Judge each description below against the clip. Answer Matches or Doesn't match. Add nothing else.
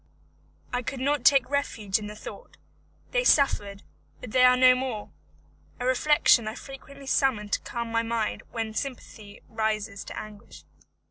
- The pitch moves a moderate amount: Matches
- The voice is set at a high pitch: Matches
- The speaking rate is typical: Matches